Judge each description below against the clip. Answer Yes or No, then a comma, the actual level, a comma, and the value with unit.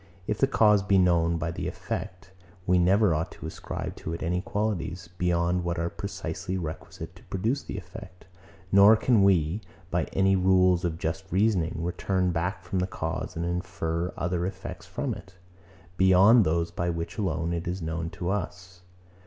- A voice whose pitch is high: No, very low, 90 Hz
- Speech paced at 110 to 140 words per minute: No, average, 180 wpm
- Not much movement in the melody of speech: Yes, narrow, 2.2 semitones